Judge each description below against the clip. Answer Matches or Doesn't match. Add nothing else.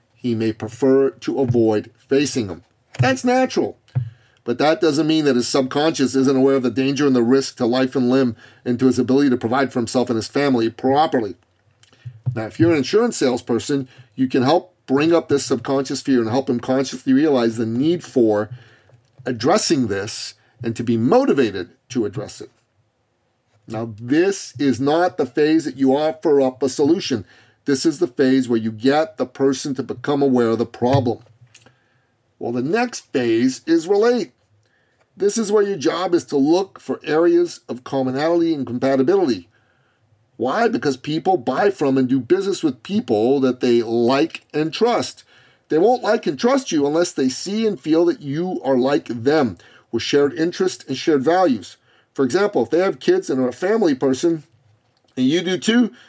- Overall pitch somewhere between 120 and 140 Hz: Matches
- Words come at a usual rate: Matches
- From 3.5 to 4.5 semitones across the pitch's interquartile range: Doesn't match